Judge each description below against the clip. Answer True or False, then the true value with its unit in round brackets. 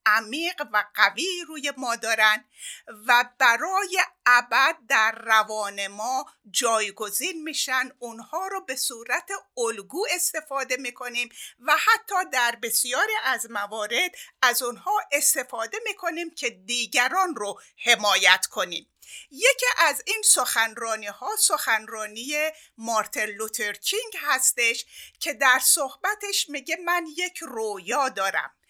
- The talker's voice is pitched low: False (255 Hz)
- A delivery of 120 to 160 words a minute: False (110 wpm)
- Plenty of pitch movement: True (7.0 semitones)